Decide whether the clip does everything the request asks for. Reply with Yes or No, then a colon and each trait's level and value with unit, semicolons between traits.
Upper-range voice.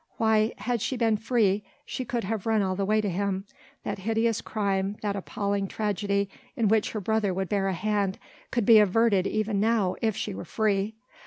Yes: high, 210 Hz